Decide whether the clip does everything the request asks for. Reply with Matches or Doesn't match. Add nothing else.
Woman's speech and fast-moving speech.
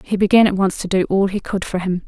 Matches